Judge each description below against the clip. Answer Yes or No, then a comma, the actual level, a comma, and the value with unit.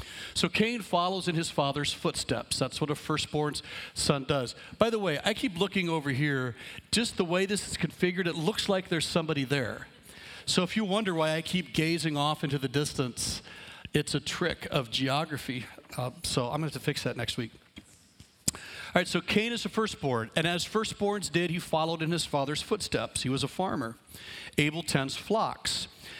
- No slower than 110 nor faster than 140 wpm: No, average, 195 wpm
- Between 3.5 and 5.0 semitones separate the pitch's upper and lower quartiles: Yes, average, 4.6 semitones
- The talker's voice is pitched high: No, medium, 160 Hz